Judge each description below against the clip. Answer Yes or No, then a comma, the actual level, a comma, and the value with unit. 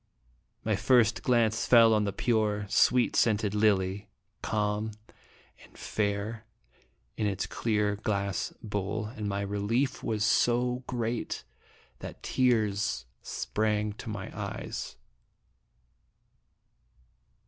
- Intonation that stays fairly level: Yes, narrow, 1.9 semitones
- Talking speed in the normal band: No, slow, 105 wpm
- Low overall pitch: Yes, low, 105 Hz